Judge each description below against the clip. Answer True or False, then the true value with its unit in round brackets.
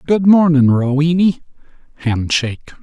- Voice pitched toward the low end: False (150 Hz)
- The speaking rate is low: True (65 wpm)